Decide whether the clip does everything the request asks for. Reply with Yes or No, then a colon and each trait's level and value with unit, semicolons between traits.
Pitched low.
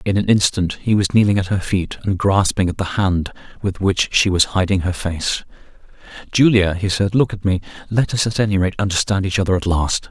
Yes: very low, 95 Hz